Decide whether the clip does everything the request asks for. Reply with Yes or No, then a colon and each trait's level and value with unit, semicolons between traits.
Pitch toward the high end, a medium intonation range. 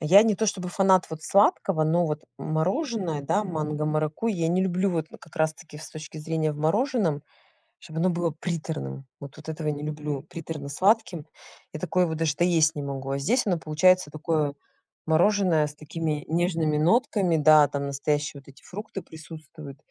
No: medium, 160 Hz; average, 3.2 semitones